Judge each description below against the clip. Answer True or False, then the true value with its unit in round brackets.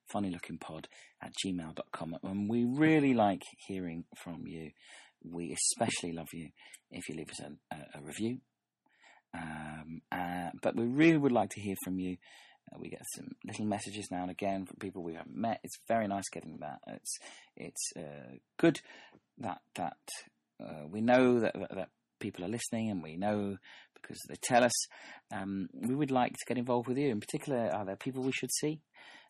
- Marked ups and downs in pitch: True (5.7 semitones)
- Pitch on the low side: True (100 Hz)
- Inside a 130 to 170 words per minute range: False (190 wpm)